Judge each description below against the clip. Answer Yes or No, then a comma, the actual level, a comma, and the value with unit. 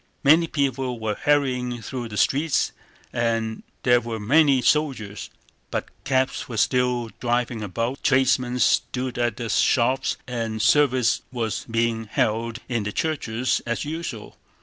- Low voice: Yes, low, 120 Hz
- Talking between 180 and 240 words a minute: No, slow, 135 wpm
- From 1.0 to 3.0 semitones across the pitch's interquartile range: Yes, narrow, 2.6 semitones